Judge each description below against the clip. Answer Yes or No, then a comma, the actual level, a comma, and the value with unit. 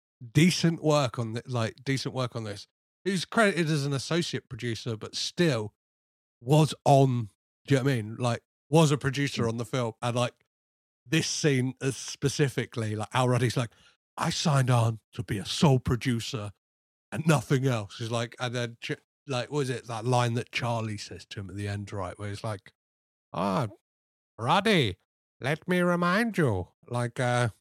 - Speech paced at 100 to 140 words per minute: No, average, 185 wpm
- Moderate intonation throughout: Yes, average, 4.6 semitones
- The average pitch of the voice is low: Yes, low, 120 Hz